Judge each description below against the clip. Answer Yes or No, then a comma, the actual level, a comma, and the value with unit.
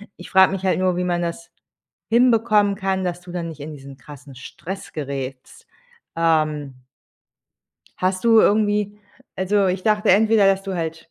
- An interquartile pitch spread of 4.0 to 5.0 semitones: Yes, average, 4.4 semitones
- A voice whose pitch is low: No, medium, 185 Hz